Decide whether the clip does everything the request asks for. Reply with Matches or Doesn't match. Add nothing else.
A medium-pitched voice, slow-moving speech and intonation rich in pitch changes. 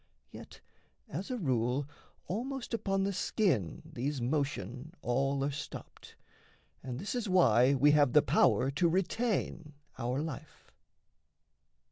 Matches